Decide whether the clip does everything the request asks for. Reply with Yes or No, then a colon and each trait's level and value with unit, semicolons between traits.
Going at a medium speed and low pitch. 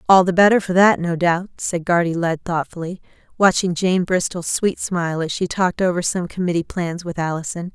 No: average, 195 wpm; medium, 175 Hz